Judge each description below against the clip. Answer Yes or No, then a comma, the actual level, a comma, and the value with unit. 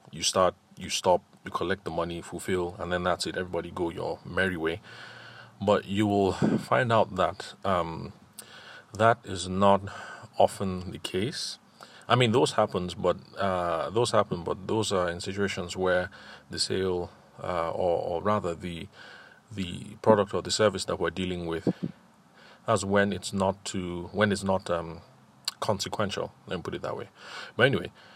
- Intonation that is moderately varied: No, narrow, 2.2 semitones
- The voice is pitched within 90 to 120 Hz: Yes, very low, 95 Hz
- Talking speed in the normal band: Yes, average, 170 wpm